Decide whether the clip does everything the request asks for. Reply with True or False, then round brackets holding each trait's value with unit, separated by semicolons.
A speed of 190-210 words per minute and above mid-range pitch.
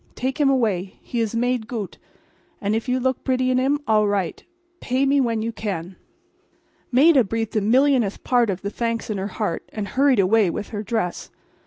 True (200 wpm; 230 Hz)